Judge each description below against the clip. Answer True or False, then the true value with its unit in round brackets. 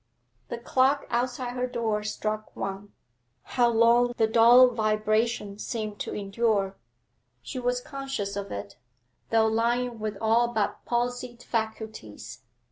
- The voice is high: True (225 Hz)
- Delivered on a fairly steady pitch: True (2.3 semitones)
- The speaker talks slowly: True (125 wpm)